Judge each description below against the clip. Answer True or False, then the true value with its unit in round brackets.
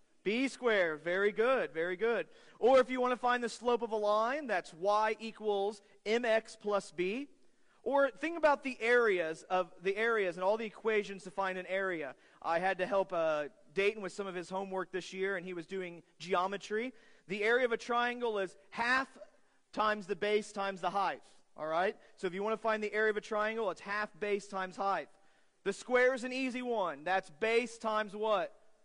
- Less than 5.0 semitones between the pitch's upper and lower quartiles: True (3.3 semitones)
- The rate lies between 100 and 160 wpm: False (205 wpm)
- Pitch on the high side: True (210 Hz)